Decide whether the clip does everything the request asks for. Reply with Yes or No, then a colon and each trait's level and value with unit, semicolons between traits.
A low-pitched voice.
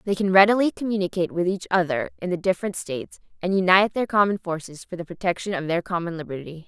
No: medium, 185 Hz